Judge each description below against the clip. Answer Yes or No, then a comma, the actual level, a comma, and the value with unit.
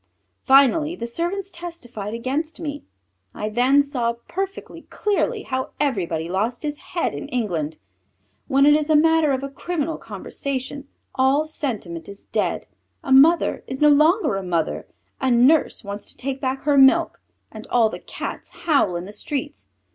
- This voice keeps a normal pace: Yes, average, 160 wpm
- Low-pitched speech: No, very high, 270 Hz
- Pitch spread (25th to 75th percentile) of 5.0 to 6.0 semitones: Yes, average, 5.3 semitones